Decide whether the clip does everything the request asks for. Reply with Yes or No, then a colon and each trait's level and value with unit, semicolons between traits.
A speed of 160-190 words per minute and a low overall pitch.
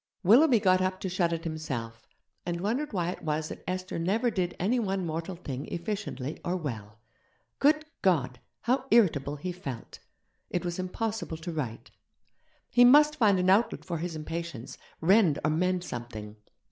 No: average, 165 wpm; medium, 175 Hz